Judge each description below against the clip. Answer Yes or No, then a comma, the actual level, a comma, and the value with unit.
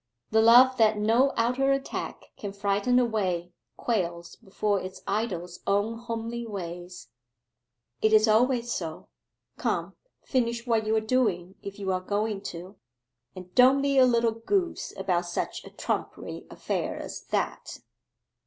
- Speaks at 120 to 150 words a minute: Yes, average, 145 wpm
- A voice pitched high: Yes, high, 215 Hz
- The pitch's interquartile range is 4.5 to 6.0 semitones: No, average, 3.9 semitones